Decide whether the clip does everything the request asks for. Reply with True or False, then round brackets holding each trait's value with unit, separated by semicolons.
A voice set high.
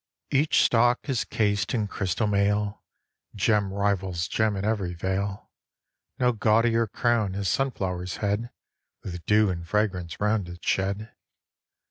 False (105 Hz)